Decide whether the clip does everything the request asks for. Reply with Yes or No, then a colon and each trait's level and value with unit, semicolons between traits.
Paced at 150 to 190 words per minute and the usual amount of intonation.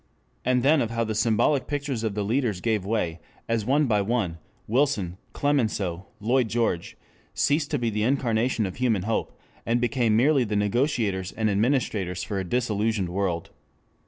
Yes: average, 165 wpm; average, 3.9 semitones